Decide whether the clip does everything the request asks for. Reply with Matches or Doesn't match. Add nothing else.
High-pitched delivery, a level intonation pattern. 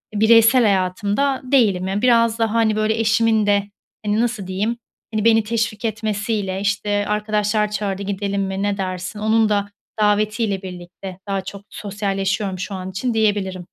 Matches